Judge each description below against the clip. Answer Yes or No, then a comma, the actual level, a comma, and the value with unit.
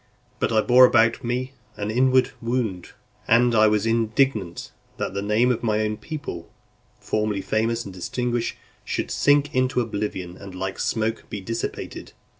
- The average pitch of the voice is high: No, low, 115 Hz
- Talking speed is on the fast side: No, average, 160 wpm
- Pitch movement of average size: Yes, average, 3.0 semitones